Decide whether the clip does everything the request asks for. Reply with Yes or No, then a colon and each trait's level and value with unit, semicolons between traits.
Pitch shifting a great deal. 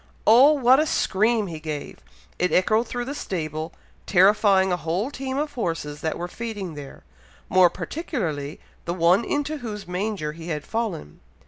Yes: wide, 6.3 semitones